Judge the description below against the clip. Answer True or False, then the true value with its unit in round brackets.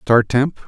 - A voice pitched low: True (125 Hz)